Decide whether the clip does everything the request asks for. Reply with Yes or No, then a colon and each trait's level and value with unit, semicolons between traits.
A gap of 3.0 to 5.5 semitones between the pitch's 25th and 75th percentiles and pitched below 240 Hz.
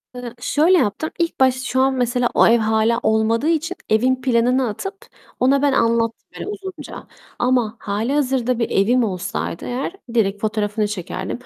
No: average, 3.5 semitones; high, 245 Hz